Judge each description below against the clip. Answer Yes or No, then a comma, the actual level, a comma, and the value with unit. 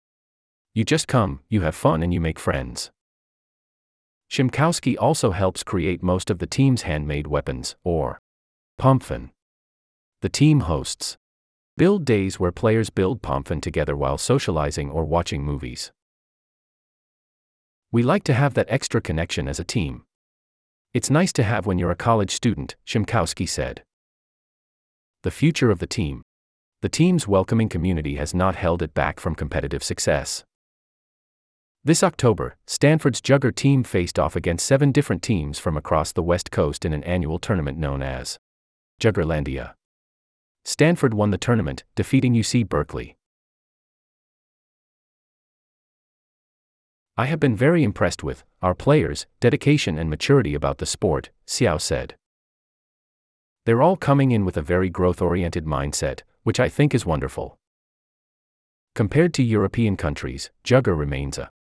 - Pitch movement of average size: No, wide, 8.8 semitones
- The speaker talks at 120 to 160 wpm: Yes, average, 140 wpm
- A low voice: Yes, very low, 90 Hz